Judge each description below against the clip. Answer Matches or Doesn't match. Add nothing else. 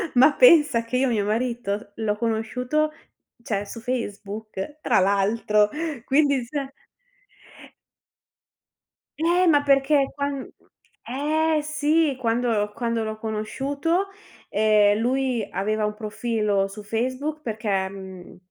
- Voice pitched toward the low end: Doesn't match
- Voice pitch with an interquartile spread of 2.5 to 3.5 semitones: Doesn't match